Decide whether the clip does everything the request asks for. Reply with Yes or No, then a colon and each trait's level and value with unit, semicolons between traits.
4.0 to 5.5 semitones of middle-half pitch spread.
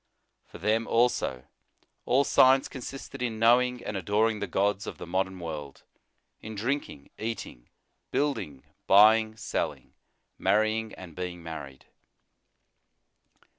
Yes: average, 4.7 semitones